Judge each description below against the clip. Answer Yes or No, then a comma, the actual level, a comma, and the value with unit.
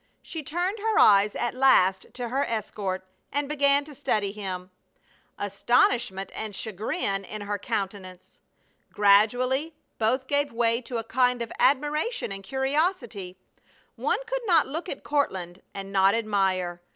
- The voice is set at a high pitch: Yes, high, 230 Hz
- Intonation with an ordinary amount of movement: No, wide, 6.2 semitones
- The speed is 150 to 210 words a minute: No, average, 140 wpm